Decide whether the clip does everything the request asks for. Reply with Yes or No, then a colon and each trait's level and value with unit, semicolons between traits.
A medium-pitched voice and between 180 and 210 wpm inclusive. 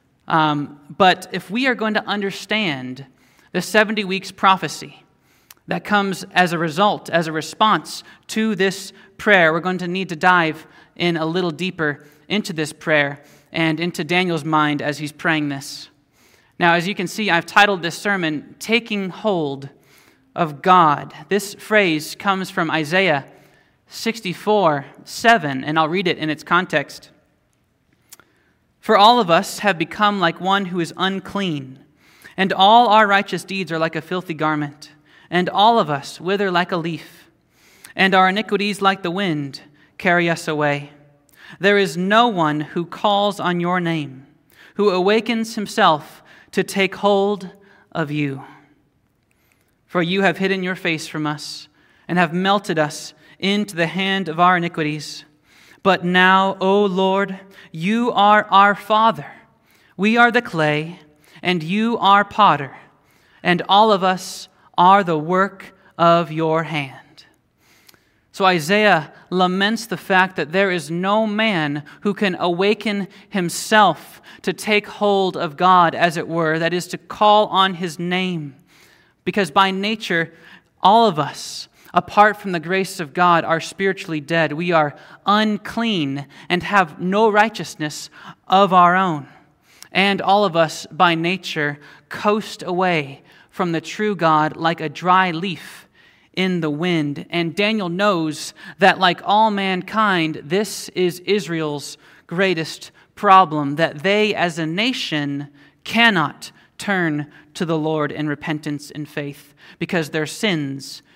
No: medium, 180 Hz; average, 145 wpm